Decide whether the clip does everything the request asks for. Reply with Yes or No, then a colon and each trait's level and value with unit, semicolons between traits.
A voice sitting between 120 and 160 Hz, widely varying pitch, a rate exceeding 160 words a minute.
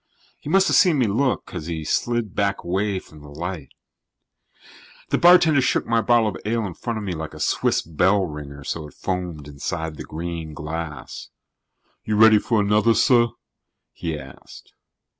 No: very low, 95 Hz; wide, 6.5 semitones; average, 175 wpm